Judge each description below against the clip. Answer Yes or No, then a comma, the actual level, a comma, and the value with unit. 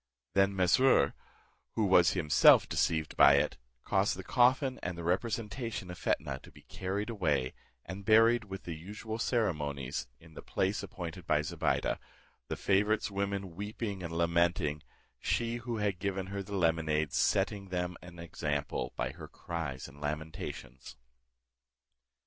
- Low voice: Yes, very low, 90 Hz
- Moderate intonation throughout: Yes, average, 4.6 semitones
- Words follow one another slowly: No, average, 145 wpm